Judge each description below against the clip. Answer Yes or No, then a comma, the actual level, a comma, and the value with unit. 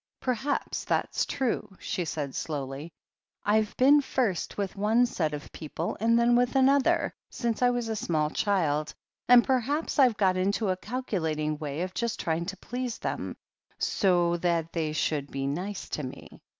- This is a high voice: Yes, high, 195 Hz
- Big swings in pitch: Yes, wide, 7.2 semitones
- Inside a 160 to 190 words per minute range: Yes, average, 165 wpm